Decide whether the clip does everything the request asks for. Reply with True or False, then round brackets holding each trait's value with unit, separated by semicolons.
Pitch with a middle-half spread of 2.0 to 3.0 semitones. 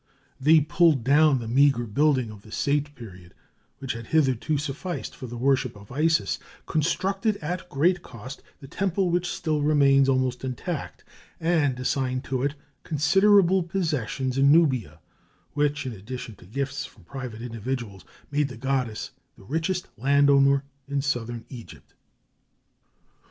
False (3.7 semitones)